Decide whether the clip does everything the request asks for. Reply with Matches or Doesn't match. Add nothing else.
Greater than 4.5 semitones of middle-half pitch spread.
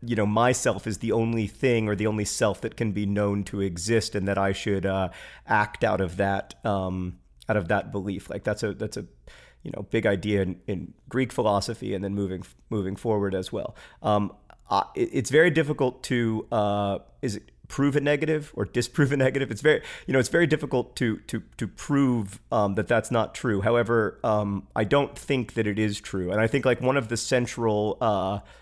Doesn't match